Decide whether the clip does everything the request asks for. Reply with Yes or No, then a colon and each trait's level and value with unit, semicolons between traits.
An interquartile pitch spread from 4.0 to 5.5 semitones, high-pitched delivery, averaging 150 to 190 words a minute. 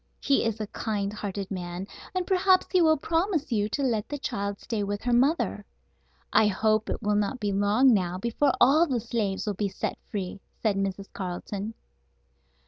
Yes: average, 4.9 semitones; high, 215 Hz; average, 185 wpm